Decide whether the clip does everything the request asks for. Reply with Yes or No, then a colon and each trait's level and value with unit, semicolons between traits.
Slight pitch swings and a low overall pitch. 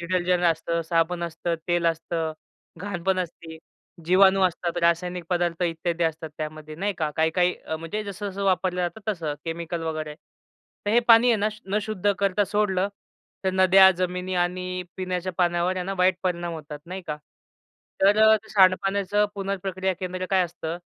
No: narrow, 2.2 semitones; medium, 180 Hz